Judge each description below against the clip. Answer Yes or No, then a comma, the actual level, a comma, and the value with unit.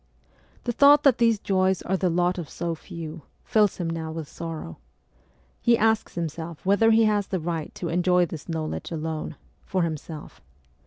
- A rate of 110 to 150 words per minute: No, average, 170 wpm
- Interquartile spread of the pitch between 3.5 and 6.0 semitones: Yes, average, 3.8 semitones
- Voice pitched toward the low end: No, medium, 175 Hz